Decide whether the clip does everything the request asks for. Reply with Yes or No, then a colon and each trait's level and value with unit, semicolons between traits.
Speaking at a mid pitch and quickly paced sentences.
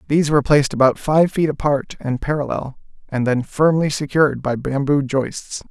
No: medium, 145 Hz; average, 170 wpm